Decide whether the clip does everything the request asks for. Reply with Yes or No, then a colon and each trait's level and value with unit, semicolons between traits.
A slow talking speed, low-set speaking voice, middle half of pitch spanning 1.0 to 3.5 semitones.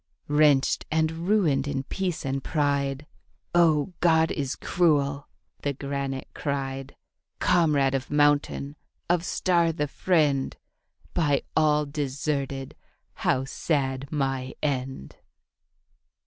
No: slow, 105 wpm; medium, 145 Hz; narrow, 2.6 semitones